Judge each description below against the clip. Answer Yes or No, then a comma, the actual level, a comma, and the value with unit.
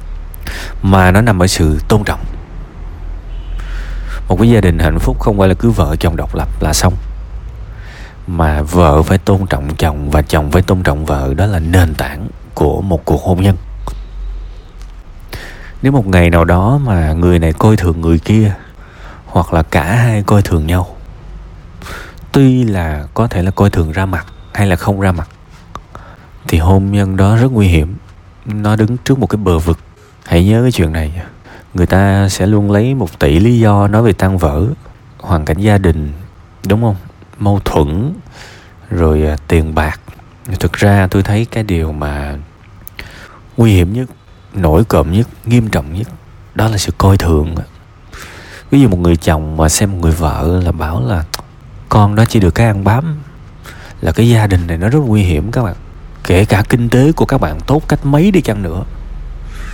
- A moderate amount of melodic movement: Yes, average, 4.3 semitones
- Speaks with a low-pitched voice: Yes, very low, 95 Hz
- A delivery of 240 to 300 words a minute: No, average, 185 wpm